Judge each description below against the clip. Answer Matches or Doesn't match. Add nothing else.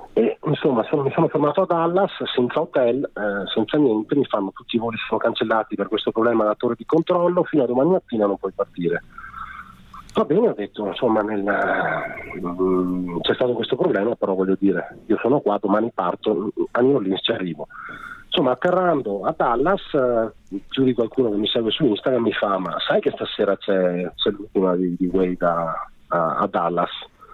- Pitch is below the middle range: Matches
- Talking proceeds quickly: Matches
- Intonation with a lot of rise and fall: Matches